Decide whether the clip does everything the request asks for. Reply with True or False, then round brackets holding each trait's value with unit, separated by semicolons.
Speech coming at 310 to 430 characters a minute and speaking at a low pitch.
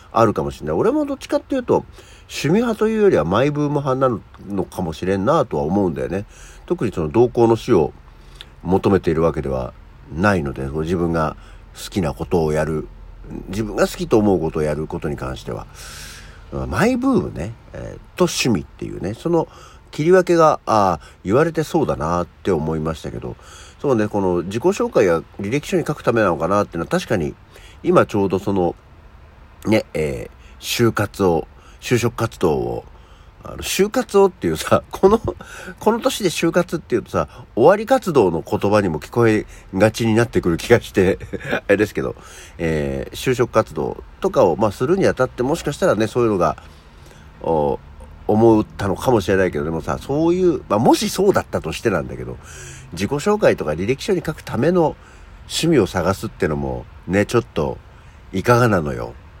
True (360 characters per minute; 105 Hz)